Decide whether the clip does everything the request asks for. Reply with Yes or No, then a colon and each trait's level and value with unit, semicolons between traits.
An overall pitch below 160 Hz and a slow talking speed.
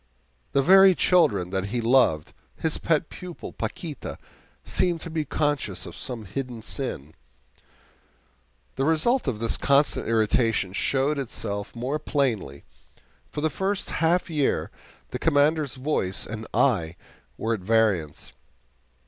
Yes: low, 135 Hz; slow, 130 wpm